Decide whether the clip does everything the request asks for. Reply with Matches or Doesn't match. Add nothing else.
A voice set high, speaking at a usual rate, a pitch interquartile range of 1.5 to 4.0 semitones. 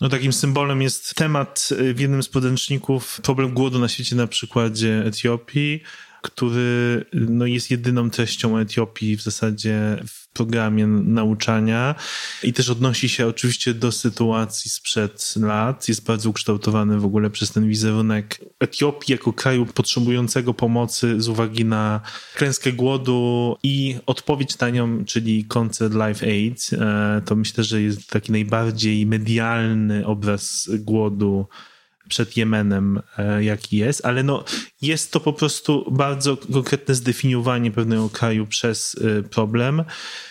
Doesn't match